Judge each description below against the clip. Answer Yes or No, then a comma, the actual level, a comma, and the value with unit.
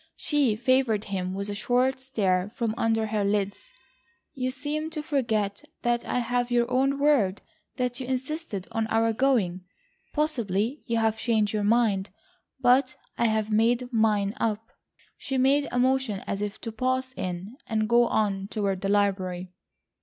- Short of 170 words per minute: Yes, average, 160 wpm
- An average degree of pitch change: Yes, average, 4.0 semitones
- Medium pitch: No, high, 225 Hz